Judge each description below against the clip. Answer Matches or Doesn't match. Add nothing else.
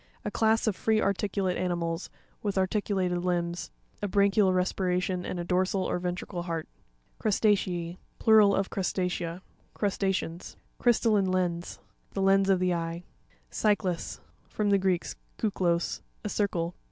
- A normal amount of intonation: Doesn't match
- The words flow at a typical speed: Doesn't match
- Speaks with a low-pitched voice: Doesn't match